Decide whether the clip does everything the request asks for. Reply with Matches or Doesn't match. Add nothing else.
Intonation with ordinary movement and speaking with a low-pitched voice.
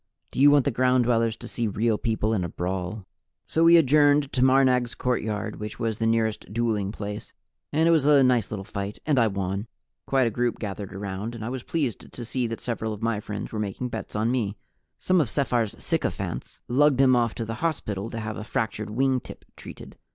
Matches